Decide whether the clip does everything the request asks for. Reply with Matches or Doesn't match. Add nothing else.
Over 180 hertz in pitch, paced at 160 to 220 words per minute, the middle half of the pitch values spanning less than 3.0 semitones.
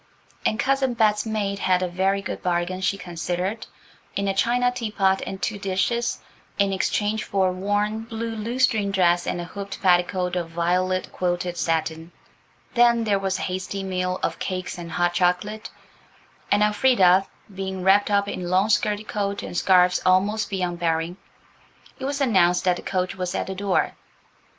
Matches